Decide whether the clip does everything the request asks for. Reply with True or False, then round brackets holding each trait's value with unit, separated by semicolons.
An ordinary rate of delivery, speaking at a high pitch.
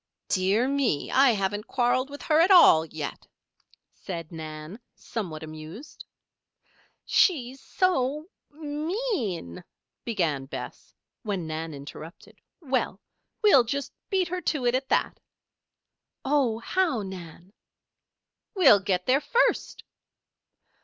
False (110 wpm; 240 Hz)